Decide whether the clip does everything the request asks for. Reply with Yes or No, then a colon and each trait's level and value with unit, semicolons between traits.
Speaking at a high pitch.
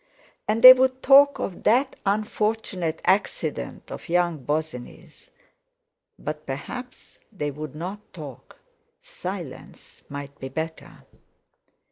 No: medium, 175 Hz